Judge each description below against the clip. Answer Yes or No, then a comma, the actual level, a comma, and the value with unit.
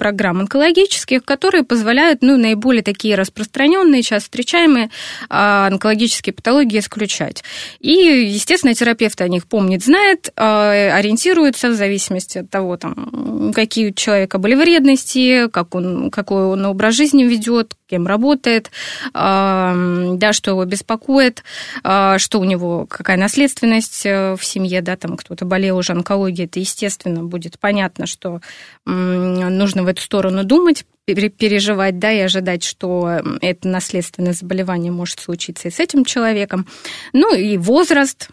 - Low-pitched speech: No, high, 205 Hz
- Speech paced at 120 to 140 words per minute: Yes, average, 130 wpm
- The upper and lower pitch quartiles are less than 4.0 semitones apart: No, average, 4.7 semitones